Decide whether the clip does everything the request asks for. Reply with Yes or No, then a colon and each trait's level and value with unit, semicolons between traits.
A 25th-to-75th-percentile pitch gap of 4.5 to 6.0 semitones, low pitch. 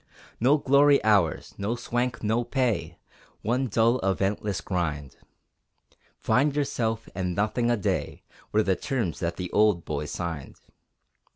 Yes: average, 5.3 semitones; low, 110 Hz